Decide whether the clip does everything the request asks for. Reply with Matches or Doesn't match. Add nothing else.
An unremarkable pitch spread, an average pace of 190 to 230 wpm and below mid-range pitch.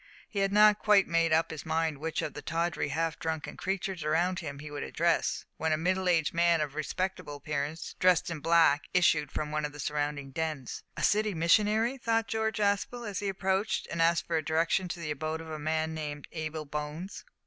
Doesn't match